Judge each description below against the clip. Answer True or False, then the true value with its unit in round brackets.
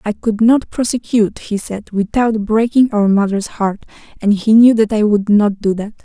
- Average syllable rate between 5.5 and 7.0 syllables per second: False (4.7 syllables/s)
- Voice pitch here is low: False (215 Hz)